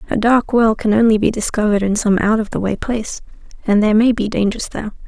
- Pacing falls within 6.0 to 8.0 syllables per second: Yes, 6.5 syllables/s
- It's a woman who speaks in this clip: Yes, female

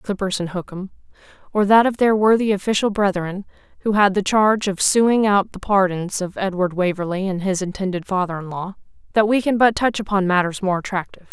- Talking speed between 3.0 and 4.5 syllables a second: No, 5.8 syllables/s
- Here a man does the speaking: No, female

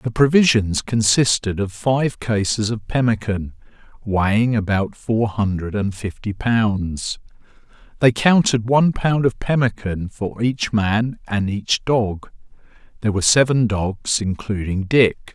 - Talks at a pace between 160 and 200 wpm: No, average, 140 wpm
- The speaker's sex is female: No, male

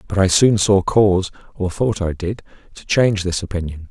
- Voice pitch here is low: Yes, very low, 95 Hz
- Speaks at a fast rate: No, average, 170 wpm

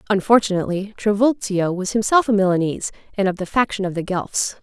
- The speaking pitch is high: Yes, high, 200 Hz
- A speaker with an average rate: Yes, average, 170 wpm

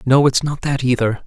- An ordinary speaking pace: No, fast, 235 wpm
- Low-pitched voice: Yes, low, 130 Hz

